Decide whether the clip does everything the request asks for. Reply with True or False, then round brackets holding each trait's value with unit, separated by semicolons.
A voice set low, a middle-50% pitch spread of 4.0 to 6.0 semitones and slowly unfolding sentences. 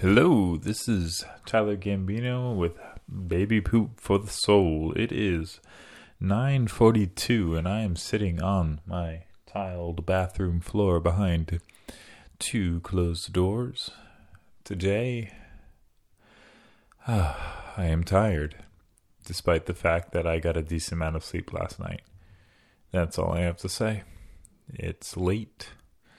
False (95 Hz; 3.6 semitones; 120 wpm)